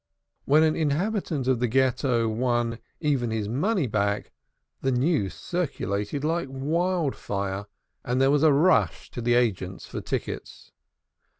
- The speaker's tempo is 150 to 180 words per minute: No, average, 140 wpm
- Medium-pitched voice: No, low, 130 Hz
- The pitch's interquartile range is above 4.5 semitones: Yes, average, 5.2 semitones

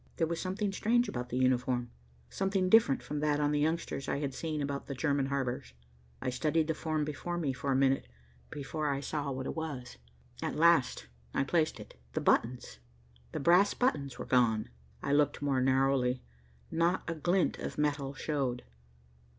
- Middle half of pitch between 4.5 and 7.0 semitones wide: No, average, 3.6 semitones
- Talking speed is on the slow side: No, average, 175 wpm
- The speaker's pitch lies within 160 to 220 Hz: No, medium, 145 Hz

